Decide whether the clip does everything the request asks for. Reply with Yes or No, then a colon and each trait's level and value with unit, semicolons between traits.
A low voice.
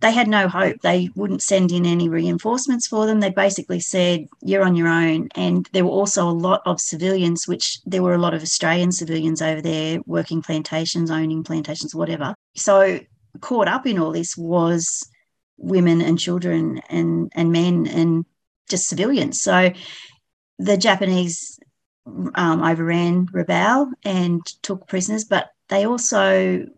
No: medium, 175 Hz